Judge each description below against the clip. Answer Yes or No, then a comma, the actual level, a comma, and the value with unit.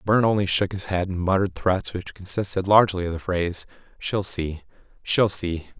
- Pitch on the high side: No, very low, 95 Hz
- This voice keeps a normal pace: Yes, average, 195 wpm